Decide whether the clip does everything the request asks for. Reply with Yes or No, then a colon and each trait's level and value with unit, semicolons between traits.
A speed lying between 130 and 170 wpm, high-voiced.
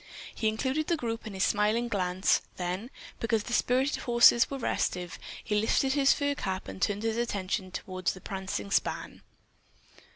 Yes: average, 165 wpm; high, 215 Hz